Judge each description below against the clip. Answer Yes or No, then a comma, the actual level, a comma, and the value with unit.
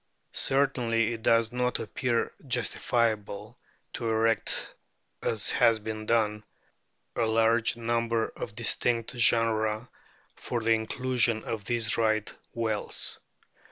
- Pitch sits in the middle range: No, low, 115 Hz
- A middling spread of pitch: No, narrow, 1.3 semitones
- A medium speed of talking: No, slow, 115 wpm